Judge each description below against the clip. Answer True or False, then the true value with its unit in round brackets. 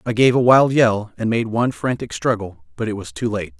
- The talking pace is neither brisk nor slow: False (250 wpm)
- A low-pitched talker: True (115 Hz)